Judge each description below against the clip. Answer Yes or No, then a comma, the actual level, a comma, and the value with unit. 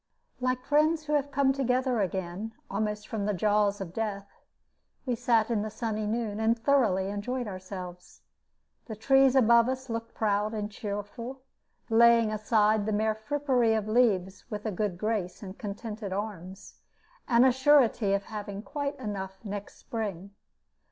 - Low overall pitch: No, high, 215 Hz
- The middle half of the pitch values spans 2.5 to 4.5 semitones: Yes, average, 3.3 semitones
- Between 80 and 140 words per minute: No, average, 155 wpm